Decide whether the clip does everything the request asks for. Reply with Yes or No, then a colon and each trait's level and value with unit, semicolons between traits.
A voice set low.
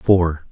Yes: very low, 85 Hz